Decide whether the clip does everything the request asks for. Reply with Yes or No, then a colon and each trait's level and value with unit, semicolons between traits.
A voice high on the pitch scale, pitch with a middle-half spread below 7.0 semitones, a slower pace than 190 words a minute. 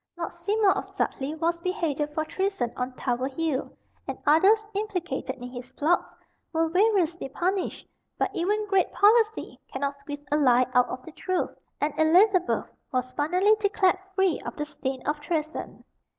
Yes: very high, 325 Hz; wide, 5.4 semitones; average, 160 wpm